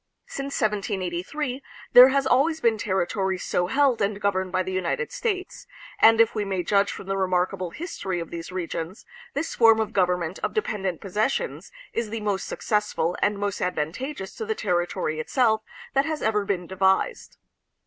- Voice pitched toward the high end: Yes, high, 200 Hz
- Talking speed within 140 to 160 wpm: No, average, 170 wpm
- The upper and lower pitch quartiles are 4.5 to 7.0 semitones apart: Yes, average, 5.1 semitones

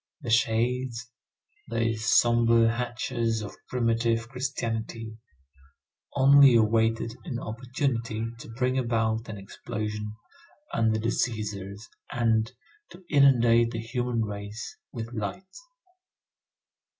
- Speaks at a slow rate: Yes, slow, 100 wpm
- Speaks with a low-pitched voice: Yes, low, 115 Hz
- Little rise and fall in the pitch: Yes, narrow, 1.7 semitones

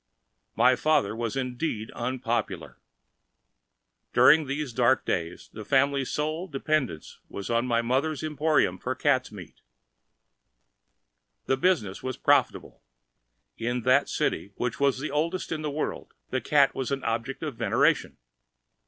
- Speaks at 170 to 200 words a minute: No, slow, 135 wpm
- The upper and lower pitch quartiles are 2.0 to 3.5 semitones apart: No, average, 4.2 semitones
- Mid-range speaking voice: No, low, 130 Hz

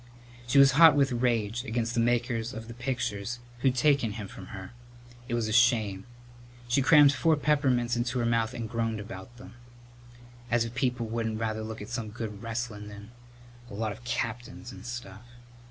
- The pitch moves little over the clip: Yes, narrow, 2.1 semitones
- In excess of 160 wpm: Yes, average, 180 wpm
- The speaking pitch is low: Yes, low, 120 Hz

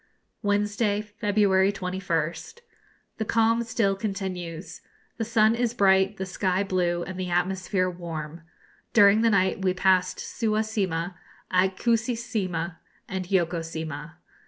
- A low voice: No, high, 190 Hz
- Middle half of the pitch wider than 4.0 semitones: No, average, 2.9 semitones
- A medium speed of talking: No, slow, 125 wpm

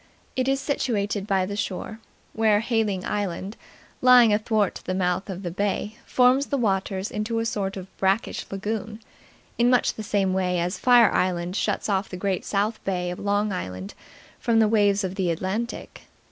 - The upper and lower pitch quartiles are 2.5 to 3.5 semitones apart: Yes, average, 2.9 semitones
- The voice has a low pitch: No, high, 205 Hz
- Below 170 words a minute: No, average, 175 wpm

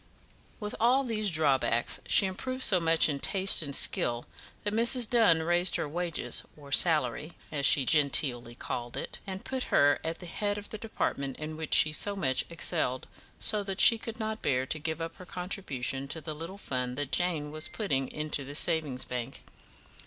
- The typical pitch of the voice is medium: Yes, medium, 160 Hz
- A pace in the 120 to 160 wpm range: No, average, 190 wpm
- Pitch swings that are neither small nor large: No, wide, 5.8 semitones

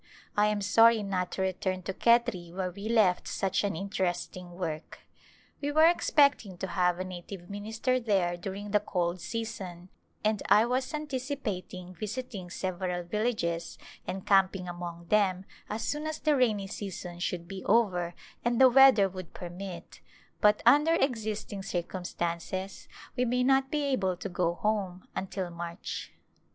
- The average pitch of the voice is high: Yes, high, 195 Hz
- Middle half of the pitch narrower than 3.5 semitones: No, average, 4.2 semitones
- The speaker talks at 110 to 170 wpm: Yes, average, 155 wpm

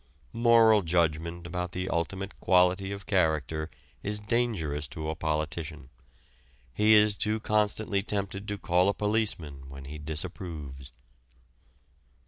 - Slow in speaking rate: Yes, slow, 120 wpm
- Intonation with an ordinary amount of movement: Yes, average, 5.0 semitones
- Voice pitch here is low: Yes, very low, 90 Hz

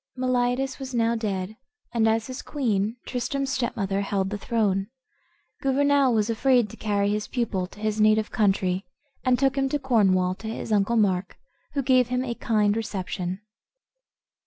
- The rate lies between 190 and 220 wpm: No, average, 160 wpm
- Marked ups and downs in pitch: No, average, 4.0 semitones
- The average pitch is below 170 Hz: No, high, 225 Hz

